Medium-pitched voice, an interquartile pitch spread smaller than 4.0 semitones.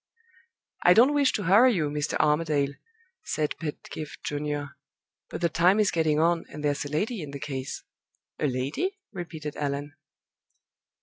Yes: medium, 155 Hz; average, 3.6 semitones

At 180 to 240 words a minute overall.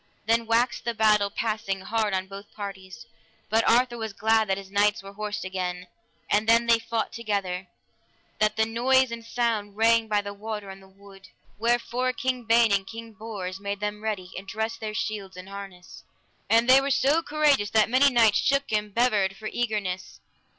Yes: average, 185 wpm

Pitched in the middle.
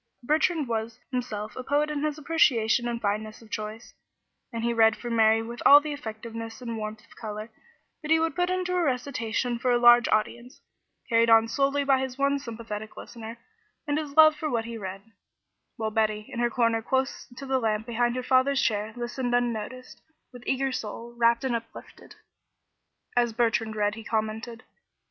No: high, 235 Hz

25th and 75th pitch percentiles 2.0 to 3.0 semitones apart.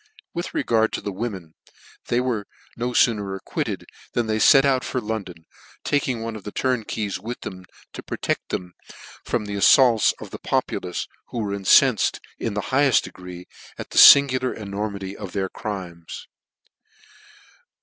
No: average, 4.0 semitones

